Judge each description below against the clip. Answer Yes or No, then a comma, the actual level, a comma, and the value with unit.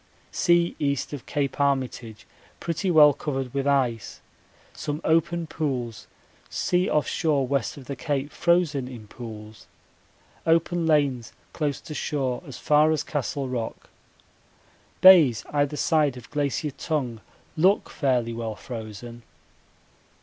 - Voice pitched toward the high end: No, medium, 140 Hz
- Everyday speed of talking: No, slow, 130 wpm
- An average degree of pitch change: Yes, average, 3.9 semitones